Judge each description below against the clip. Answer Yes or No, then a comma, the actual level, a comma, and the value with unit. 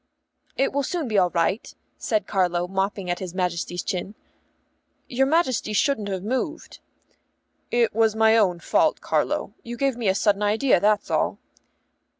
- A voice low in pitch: No, high, 210 Hz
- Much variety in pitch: No, average, 4.3 semitones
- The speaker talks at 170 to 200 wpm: No, average, 155 wpm